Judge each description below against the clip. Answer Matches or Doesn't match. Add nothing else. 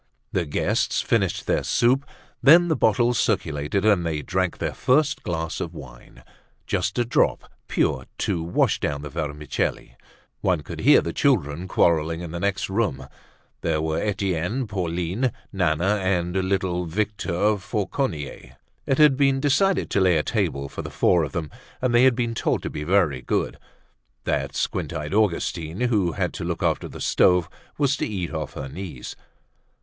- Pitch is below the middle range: Matches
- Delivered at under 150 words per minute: Doesn't match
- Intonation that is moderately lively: Doesn't match